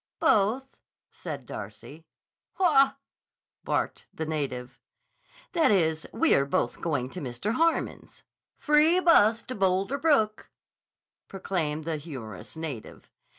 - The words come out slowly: Yes, slow, 110 wpm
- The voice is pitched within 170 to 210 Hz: Yes, high, 190 Hz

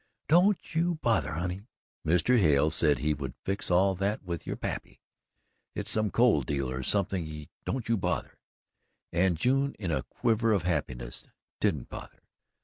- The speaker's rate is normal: Yes, average, 155 wpm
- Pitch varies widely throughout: Yes, wide, 6.6 semitones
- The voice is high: No, very low, 90 Hz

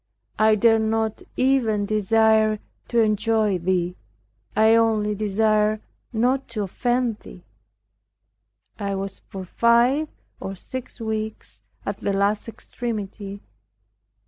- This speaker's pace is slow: Yes, slow, 110 wpm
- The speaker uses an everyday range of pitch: No, narrow, 2.0 semitones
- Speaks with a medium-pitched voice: No, high, 215 Hz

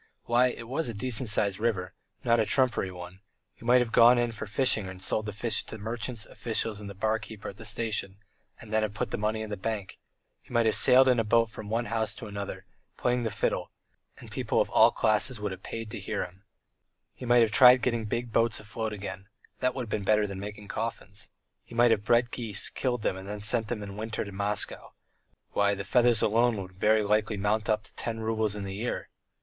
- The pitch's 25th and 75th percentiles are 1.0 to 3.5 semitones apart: Yes, narrow, 2.4 semitones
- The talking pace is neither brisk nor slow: No, fast, 230 wpm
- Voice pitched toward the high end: No, low, 110 Hz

